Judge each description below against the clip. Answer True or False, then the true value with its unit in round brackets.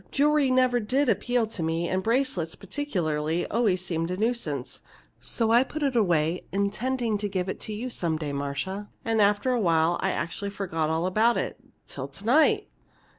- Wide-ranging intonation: True (6.4 semitones)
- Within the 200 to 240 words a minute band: False (180 wpm)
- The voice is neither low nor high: False (200 Hz)